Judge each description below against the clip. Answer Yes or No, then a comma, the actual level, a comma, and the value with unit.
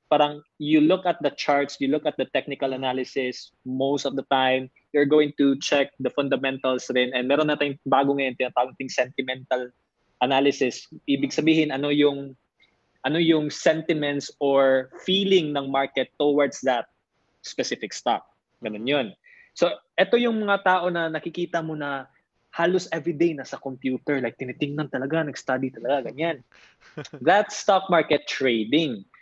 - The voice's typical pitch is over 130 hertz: Yes, medium, 140 Hz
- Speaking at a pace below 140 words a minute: No, average, 150 wpm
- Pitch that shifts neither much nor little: Yes, average, 3.3 semitones